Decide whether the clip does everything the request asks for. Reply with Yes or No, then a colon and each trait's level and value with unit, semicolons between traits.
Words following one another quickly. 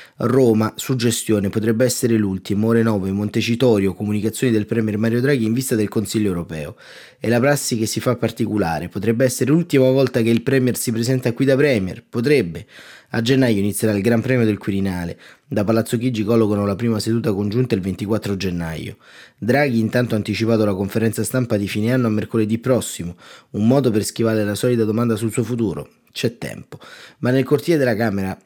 Yes: fast, 185 wpm